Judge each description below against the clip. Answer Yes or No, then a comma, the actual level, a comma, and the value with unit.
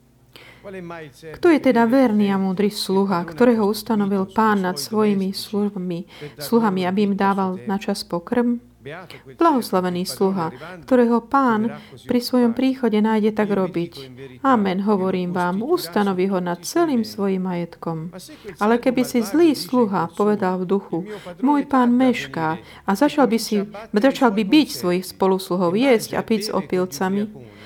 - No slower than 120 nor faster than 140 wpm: Yes, average, 135 wpm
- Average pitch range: Yes, average, 4.5 semitones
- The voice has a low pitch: No, high, 200 Hz